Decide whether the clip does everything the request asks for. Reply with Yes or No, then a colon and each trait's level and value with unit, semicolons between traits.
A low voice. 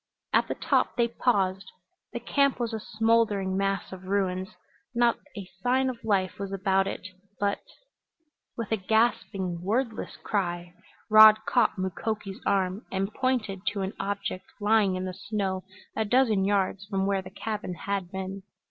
No: high, 200 Hz